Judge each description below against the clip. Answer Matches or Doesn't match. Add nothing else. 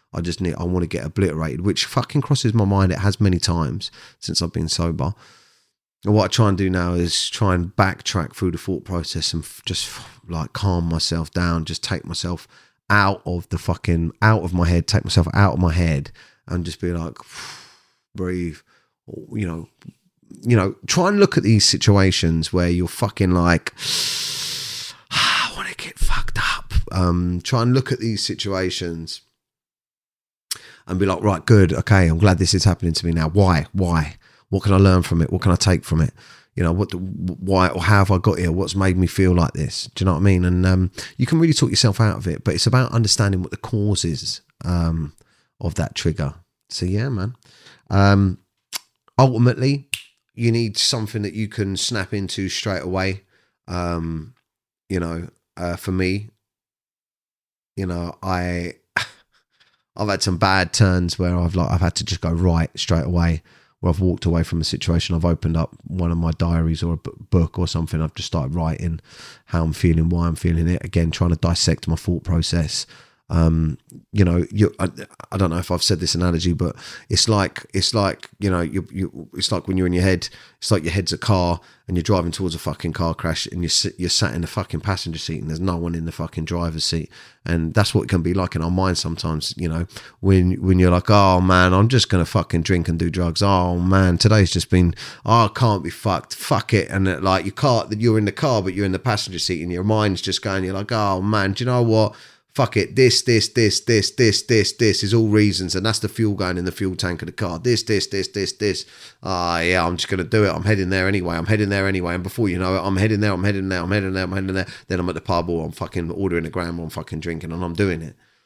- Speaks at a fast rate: Matches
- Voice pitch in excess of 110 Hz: Doesn't match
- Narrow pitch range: Doesn't match